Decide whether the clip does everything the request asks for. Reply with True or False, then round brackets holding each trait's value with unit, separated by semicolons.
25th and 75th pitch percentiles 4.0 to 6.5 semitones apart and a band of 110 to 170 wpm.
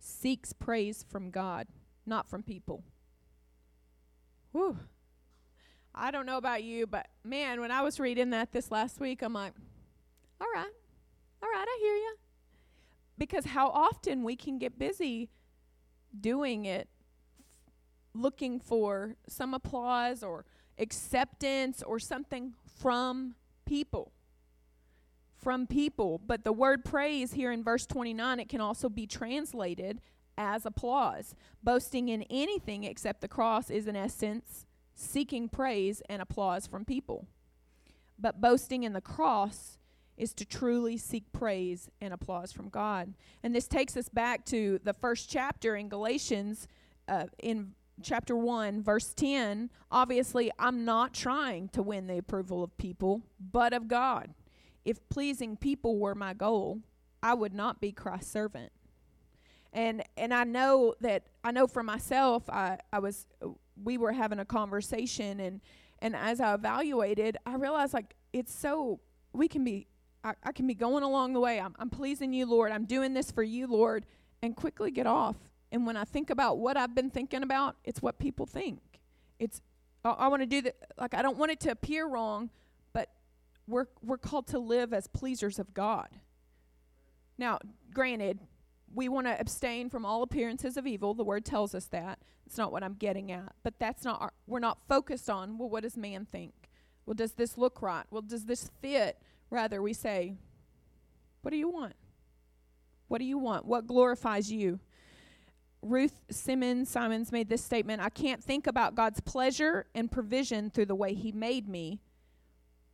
True (4.5 semitones; 165 wpm)